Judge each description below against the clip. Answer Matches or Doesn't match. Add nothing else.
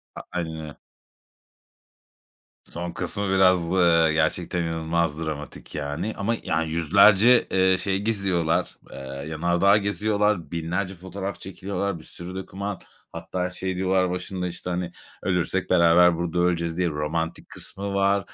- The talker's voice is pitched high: Doesn't match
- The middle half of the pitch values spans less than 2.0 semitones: Doesn't match